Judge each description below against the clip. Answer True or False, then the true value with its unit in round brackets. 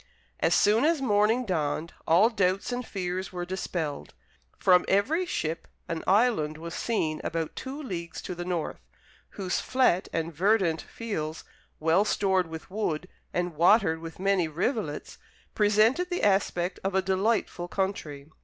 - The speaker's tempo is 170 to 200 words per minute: False (145 wpm)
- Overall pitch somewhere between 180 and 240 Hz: True (185 Hz)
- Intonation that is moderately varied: True (4.4 semitones)